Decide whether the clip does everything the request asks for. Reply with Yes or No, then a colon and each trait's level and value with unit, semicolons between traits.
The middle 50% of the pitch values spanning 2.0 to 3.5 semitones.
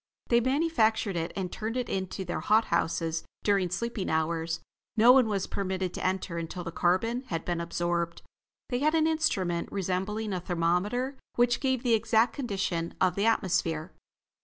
No: average, 5.2 semitones